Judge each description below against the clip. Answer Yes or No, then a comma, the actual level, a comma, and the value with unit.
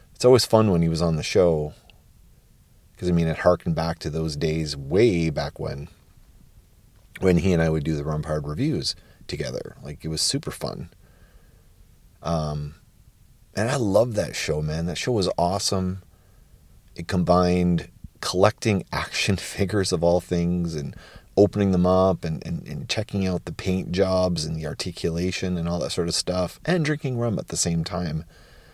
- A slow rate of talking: No, average, 175 wpm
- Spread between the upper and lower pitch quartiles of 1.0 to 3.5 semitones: Yes, average, 3.0 semitones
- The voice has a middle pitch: No, very low, 90 Hz